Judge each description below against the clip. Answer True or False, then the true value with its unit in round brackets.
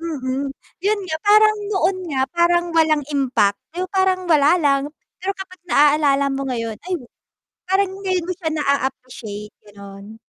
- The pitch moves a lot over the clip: True (5.9 semitones)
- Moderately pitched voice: False (305 Hz)